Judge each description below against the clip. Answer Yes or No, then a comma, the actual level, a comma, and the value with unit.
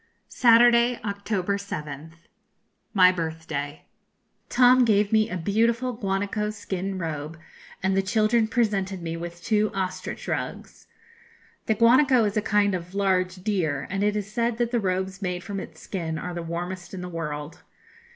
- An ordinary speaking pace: Yes, average, 160 wpm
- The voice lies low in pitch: No, high, 195 Hz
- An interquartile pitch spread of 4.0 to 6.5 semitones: No, average, 3.6 semitones